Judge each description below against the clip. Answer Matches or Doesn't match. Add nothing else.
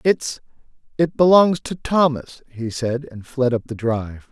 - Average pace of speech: Matches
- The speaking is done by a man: Matches